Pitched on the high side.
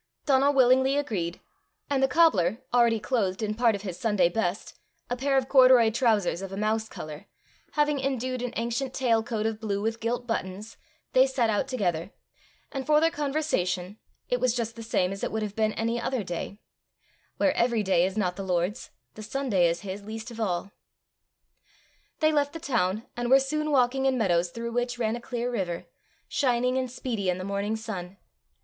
Yes: high, 225 Hz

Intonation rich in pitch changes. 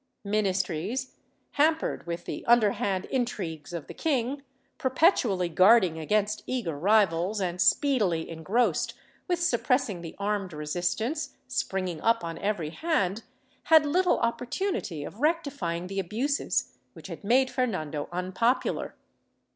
Yes: wide, 6.7 semitones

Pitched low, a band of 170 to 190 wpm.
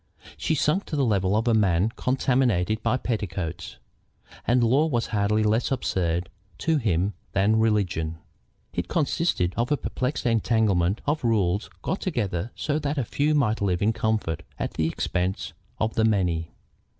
No: low, 110 Hz; average, 160 wpm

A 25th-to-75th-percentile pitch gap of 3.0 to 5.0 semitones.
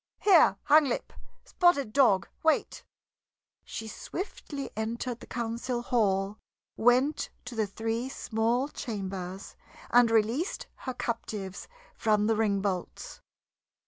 Yes: average, 3.5 semitones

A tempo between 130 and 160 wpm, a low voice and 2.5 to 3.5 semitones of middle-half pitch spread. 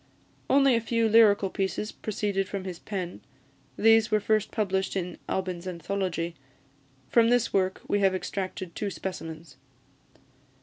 No: slow, 135 wpm; high, 195 Hz; average, 2.8 semitones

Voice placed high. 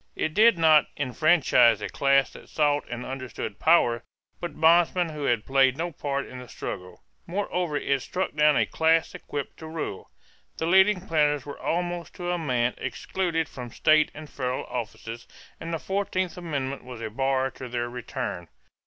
No: medium, 145 Hz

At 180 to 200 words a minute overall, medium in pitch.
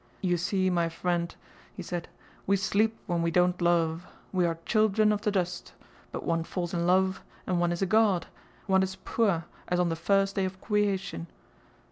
Yes: average, 190 wpm; medium, 180 Hz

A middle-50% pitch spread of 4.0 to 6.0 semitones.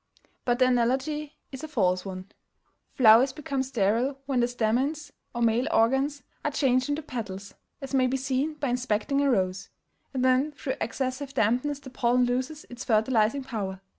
No: average, 3.3 semitones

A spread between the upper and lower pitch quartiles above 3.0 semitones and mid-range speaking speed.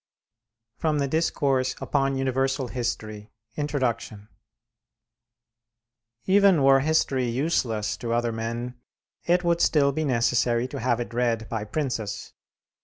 No: average, 3.5 semitones; slow, 115 wpm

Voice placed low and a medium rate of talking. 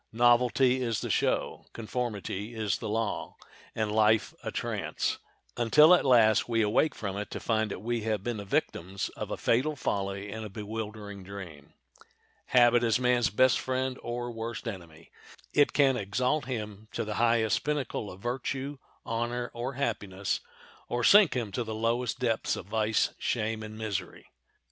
Yes: low, 115 Hz; average, 165 wpm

